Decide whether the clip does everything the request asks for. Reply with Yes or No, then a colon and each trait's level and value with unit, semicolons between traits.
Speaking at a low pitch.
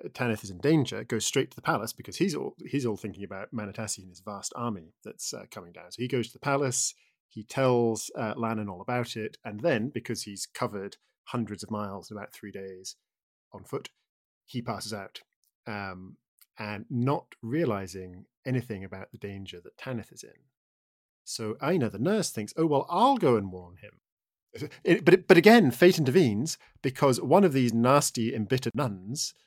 Yes: low, 115 Hz